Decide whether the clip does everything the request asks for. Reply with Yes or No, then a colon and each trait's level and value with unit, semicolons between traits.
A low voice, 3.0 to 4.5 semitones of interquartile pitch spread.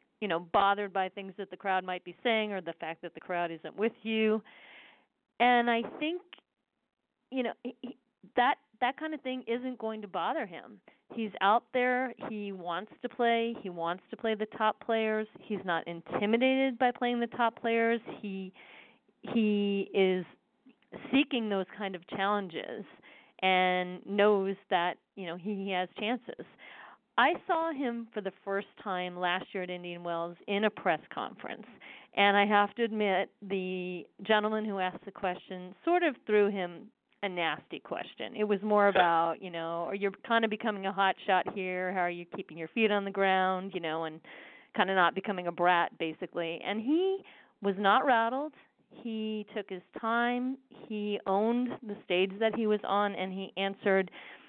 No: high, 205 Hz; average, 3.7 semitones